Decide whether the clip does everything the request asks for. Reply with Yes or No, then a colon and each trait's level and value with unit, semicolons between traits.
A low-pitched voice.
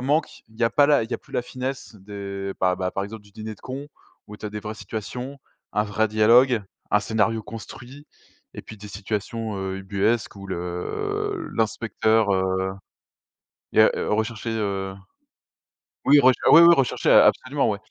Yes: low, 110 Hz